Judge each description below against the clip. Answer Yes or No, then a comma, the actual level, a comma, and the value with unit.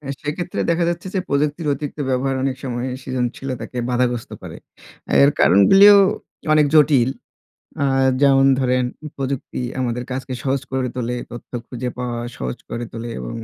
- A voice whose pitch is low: Yes, low, 130 Hz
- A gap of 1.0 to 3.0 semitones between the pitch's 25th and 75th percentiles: Yes, average, 2.7 semitones